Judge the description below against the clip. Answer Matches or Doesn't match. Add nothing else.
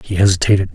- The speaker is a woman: Doesn't match